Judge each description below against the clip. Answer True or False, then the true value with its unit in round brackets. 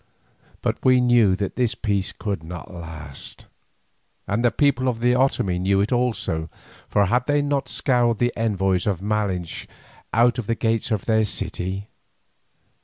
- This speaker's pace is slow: False (160 wpm)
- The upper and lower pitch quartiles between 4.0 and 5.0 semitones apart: True (4.3 semitones)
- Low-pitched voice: True (110 Hz)